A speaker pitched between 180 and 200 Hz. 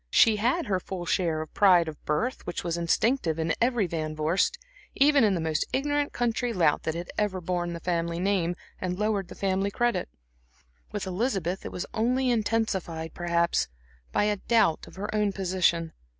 Yes: high, 190 Hz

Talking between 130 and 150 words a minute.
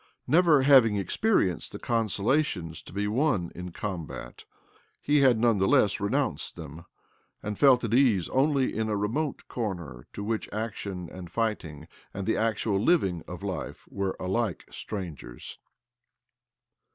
Yes: average, 140 wpm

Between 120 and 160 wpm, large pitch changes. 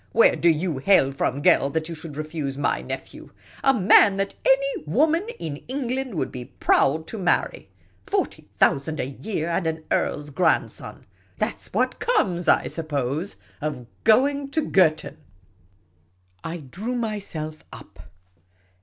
Yes: average, 150 wpm; wide, 7.3 semitones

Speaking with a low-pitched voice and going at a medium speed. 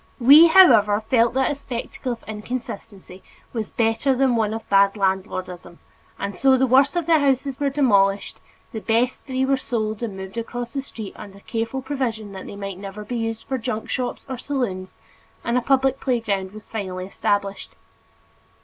No: high, 230 Hz; average, 175 wpm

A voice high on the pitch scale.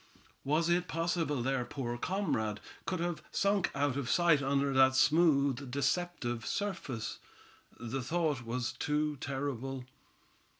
No: medium, 140 Hz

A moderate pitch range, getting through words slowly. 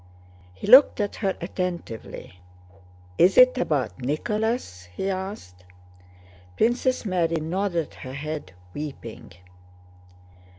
No: wide, 6.7 semitones; slow, 95 wpm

